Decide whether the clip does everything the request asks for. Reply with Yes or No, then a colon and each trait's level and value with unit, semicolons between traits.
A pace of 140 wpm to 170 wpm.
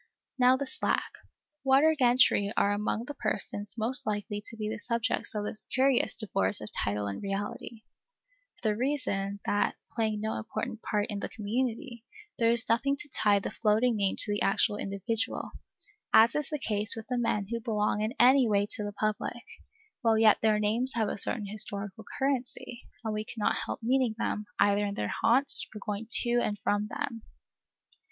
No: average, 185 wpm